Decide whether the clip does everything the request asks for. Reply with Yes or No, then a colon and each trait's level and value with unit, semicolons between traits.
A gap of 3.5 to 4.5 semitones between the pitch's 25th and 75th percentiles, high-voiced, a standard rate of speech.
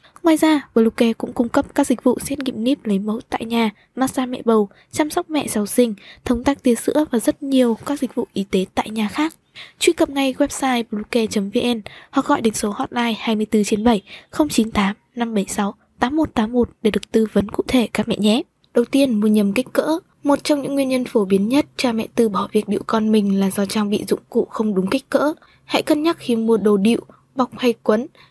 Yes: average, 4.1 semitones; high, 240 Hz; average, 225 wpm